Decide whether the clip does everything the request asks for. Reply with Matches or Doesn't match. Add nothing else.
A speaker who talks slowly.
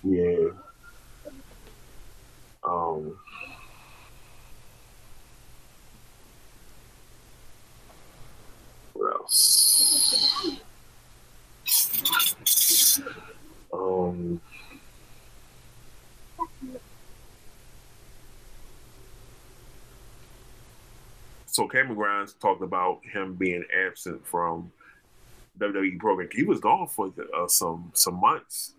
Matches